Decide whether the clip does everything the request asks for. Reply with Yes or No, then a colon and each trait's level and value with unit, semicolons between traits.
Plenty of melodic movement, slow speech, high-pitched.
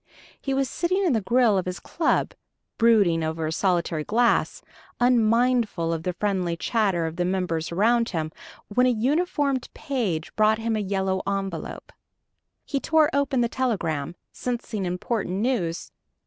No: wide, 5.8 semitones; average, 150 wpm; high, 215 Hz